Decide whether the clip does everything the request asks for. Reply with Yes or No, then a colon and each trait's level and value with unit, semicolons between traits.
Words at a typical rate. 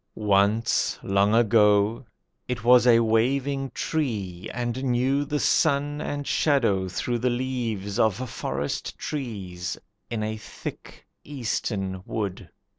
No: slow, 115 wpm